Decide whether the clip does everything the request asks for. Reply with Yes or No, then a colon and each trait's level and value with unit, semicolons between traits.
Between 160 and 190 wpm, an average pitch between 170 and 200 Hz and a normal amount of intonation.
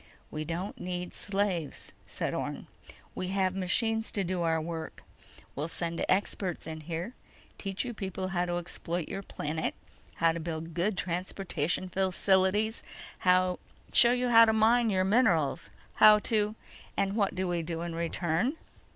No: average, 150 wpm; medium, 185 Hz; average, 3.3 semitones